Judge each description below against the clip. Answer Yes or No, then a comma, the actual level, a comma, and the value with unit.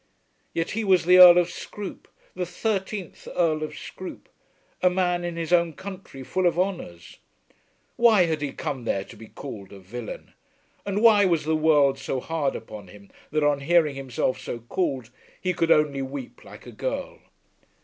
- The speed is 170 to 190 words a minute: Yes, average, 180 wpm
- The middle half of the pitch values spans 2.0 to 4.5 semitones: No, average, 5.1 semitones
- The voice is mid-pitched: Yes, medium, 160 Hz